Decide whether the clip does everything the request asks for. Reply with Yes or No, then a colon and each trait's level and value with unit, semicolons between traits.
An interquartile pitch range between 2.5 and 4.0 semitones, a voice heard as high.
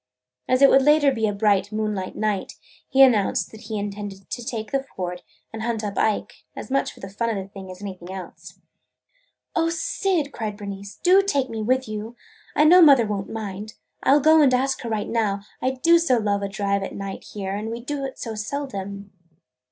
No: average, 5.0 semitones; high, 220 Hz